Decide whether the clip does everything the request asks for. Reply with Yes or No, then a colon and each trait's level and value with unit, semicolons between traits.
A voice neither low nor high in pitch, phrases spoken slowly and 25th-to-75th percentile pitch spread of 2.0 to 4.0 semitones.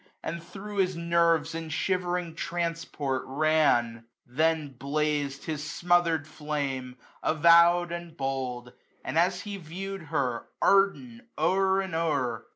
Yes: medium, 165 Hz; slow, 125 wpm; average, 3.6 semitones